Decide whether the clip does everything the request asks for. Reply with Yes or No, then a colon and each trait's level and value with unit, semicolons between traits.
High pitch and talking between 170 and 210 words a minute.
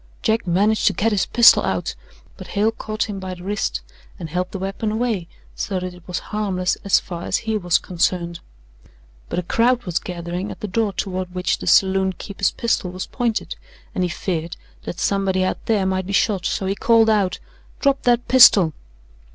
Yes: high, 195 Hz; average, 195 wpm